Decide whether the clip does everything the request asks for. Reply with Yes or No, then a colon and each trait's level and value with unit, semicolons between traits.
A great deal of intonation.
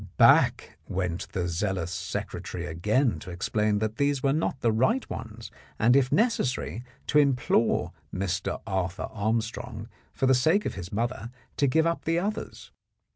Yes: wide, 6.1 semitones